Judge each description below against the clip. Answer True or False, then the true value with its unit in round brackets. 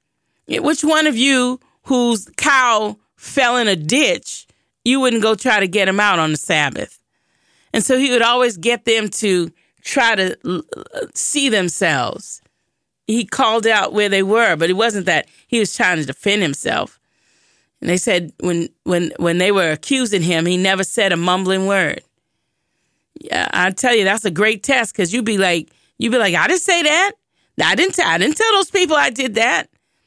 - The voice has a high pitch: True (220 Hz)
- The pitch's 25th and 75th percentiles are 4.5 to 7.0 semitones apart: True (5.3 semitones)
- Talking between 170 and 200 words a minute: True (190 wpm)